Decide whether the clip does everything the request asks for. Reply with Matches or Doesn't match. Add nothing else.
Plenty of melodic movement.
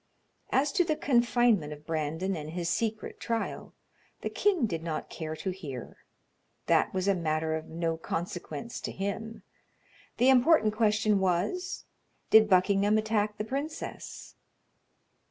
Matches